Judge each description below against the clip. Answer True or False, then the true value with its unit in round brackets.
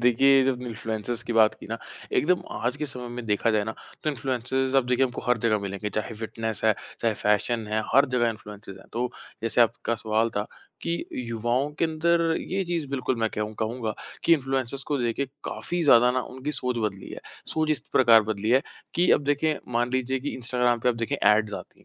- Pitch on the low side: True (120 Hz)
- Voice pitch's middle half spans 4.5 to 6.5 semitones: False (3.3 semitones)